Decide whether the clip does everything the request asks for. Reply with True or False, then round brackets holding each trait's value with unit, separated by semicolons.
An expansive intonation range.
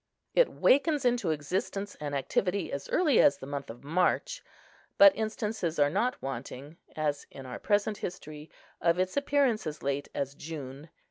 True (7.3 semitones)